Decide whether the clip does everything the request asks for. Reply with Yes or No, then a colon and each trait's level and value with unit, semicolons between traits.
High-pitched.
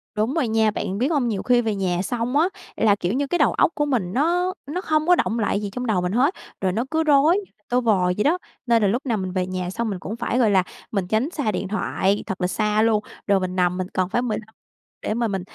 Yes: high, 220 Hz